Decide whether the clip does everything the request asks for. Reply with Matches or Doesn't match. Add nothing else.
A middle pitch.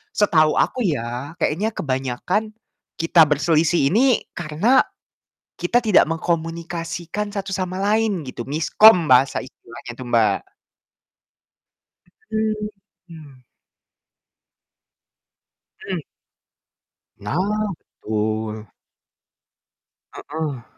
Matches